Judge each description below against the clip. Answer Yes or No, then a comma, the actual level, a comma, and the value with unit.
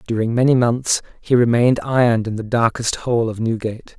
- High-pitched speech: No, low, 115 Hz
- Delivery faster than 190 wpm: No, average, 180 wpm